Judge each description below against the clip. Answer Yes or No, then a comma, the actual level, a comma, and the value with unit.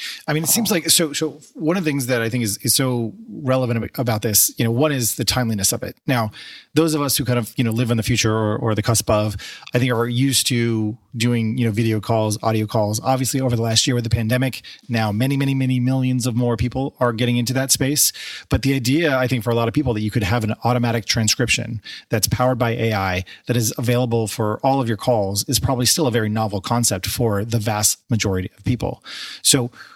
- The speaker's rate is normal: No, fast, 245 wpm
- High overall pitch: No, low, 120 Hz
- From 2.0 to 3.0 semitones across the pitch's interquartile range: Yes, average, 2.7 semitones